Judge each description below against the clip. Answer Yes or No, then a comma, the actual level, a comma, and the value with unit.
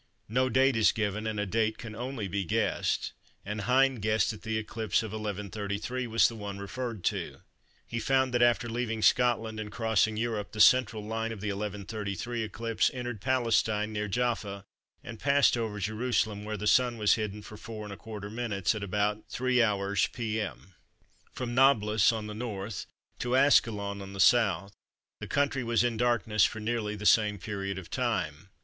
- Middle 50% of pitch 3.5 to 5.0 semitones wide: No, narrow, 2.5 semitones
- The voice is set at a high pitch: No, low, 110 Hz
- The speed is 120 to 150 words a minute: No, average, 170 wpm